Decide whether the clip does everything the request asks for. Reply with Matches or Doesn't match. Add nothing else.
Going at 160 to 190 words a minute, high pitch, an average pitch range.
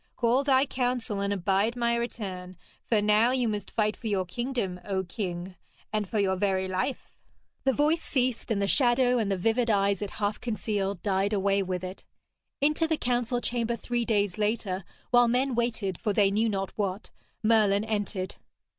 Matches